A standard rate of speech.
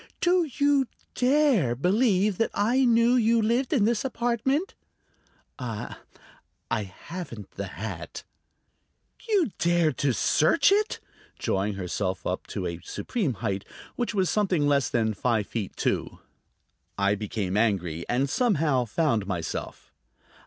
No: slow, 125 wpm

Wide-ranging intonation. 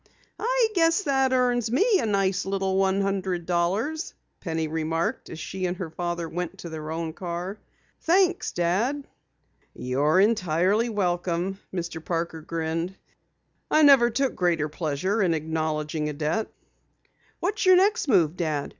Yes: wide, 6.2 semitones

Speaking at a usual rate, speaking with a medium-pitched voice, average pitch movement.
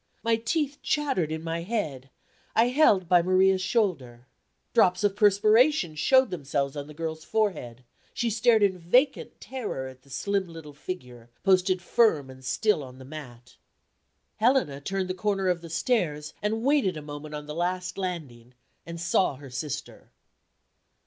No: average, 160 wpm; medium, 180 Hz; wide, 6.4 semitones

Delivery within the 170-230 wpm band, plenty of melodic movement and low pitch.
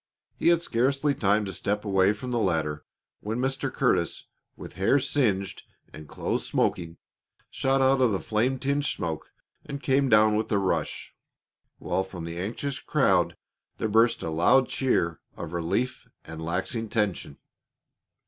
No: average, 155 wpm; wide, 6.1 semitones; low, 105 Hz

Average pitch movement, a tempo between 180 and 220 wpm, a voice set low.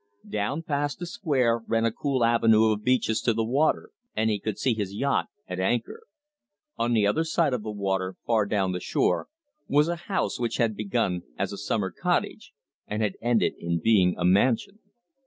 Yes: average, 4.4 semitones; average, 195 wpm; low, 115 Hz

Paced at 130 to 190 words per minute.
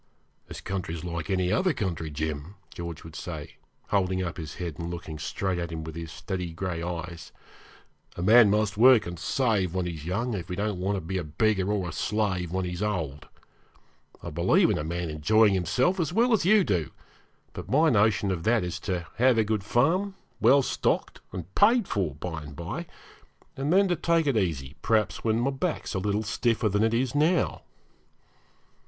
No: average, 200 wpm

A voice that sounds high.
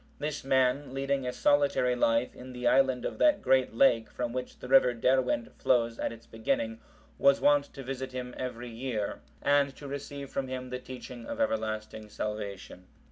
No: low, 125 Hz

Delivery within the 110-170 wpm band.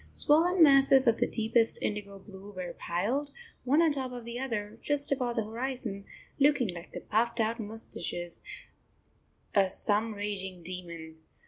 Yes: average, 150 wpm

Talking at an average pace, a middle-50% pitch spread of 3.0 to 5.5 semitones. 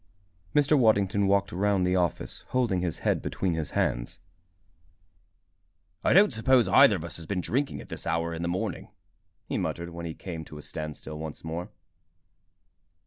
Yes: average, 170 wpm; average, 4.3 semitones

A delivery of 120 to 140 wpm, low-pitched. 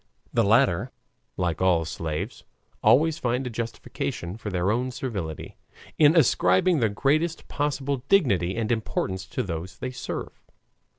Yes: slow, 135 wpm; low, 115 Hz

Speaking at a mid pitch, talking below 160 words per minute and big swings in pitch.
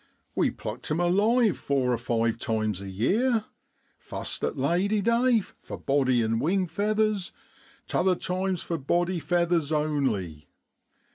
Yes: medium, 170 Hz; slow, 135 wpm; wide, 7.9 semitones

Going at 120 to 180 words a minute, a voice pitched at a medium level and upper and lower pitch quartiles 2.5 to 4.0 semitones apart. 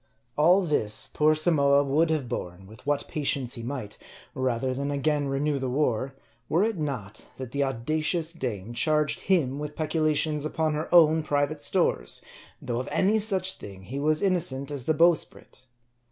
Yes: average, 170 wpm; medium, 145 Hz; average, 3.3 semitones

